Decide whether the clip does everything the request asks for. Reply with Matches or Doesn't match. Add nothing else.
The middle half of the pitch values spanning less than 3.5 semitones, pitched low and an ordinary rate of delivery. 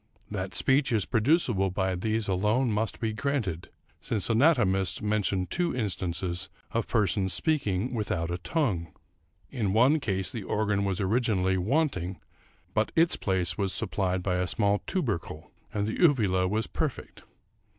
Doesn't match